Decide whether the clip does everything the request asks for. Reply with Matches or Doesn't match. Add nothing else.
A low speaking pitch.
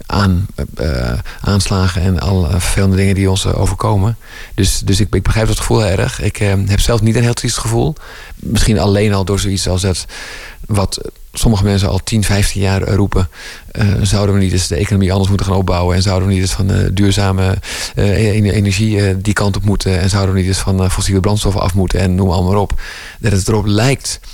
Matches